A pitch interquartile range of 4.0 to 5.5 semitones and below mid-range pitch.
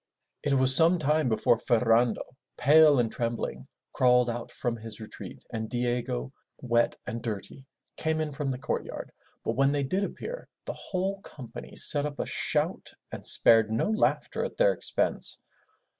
Yes: average, 4.4 semitones; low, 125 Hz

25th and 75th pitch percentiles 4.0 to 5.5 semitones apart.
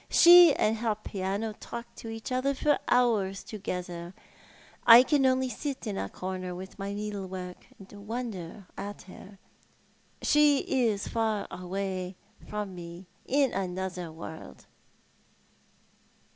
Yes: average, 4.3 semitones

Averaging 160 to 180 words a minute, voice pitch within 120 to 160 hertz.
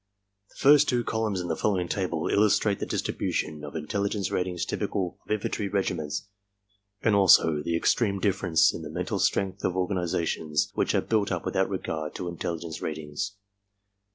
No: average, 165 wpm; very low, 95 Hz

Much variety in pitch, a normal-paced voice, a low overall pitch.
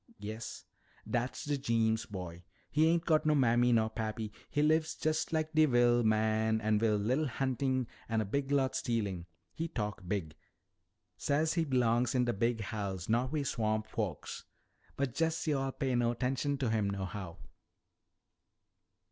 No: average, 4.5 semitones; average, 160 wpm; low, 120 Hz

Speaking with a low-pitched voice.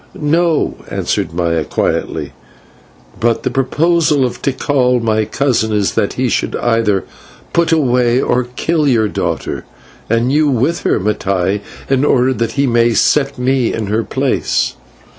Yes: low, 125 Hz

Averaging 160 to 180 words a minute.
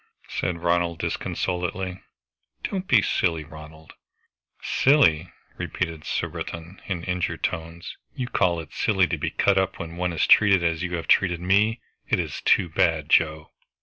No: average, 150 wpm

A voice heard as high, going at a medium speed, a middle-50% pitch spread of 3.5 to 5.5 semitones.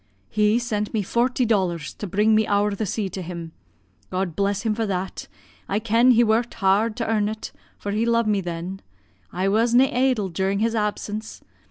No: high, 210 Hz; average, 195 wpm; average, 2.8 semitones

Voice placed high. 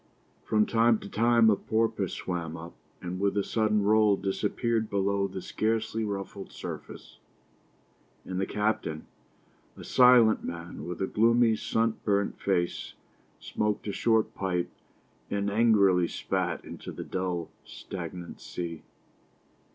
No: low, 100 Hz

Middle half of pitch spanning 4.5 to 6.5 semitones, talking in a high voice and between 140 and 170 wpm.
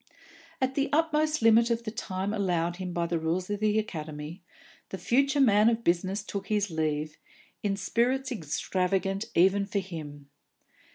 Yes: average, 5.1 semitones; high, 195 Hz; average, 160 wpm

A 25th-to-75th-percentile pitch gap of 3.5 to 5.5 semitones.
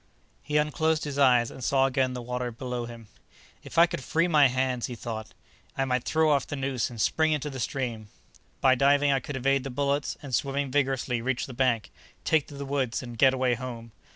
No: narrow, 2.4 semitones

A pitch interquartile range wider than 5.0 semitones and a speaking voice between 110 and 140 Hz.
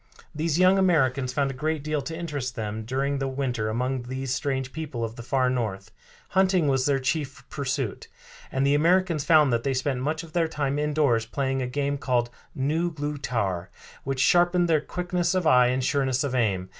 No: average, 3.4 semitones; low, 135 Hz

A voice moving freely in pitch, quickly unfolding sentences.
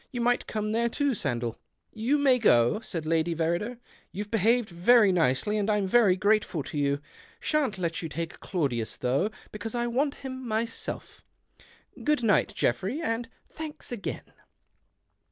No: wide, 6.3 semitones; average, 155 wpm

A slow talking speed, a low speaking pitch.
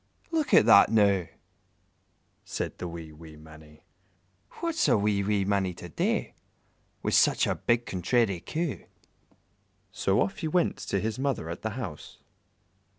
No: average, 150 wpm; low, 100 Hz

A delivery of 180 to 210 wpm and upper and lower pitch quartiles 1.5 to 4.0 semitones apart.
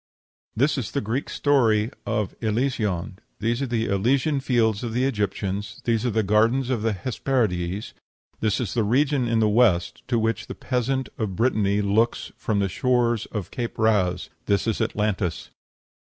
No: average, 170 wpm; average, 3.3 semitones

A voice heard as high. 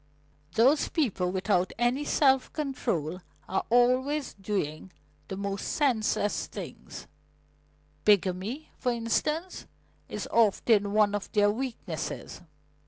Yes: high, 220 Hz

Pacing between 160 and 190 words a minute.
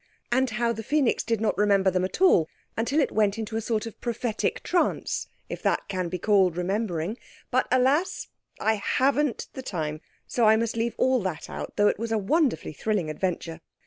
Yes: average, 185 wpm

